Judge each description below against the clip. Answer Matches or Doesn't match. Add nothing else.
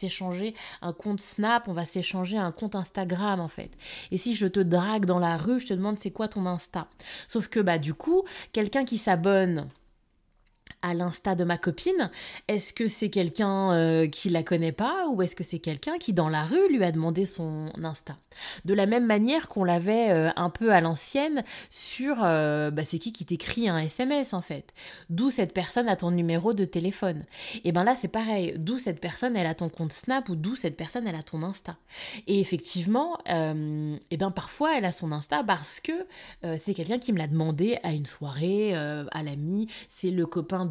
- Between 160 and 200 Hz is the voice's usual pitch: Matches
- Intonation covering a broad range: Doesn't match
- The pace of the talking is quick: Doesn't match